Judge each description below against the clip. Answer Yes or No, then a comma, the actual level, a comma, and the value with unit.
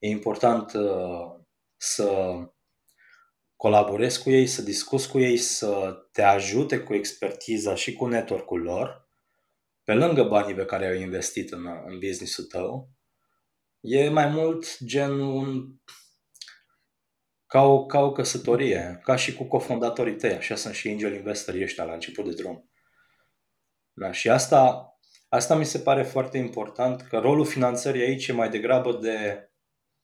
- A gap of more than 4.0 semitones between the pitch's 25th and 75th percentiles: Yes, average, 4.7 semitones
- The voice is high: No, low, 125 Hz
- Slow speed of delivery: No, average, 140 wpm